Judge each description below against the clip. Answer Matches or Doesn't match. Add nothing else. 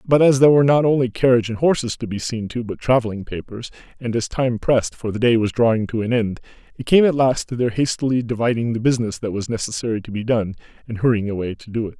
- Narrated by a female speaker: Doesn't match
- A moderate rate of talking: Doesn't match